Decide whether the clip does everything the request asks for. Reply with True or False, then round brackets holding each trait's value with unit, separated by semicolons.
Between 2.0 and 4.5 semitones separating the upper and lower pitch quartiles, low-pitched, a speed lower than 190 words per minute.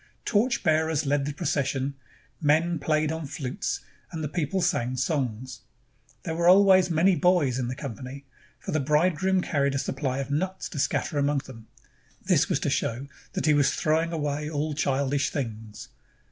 False (3.4 semitones; 145 Hz; 170 wpm)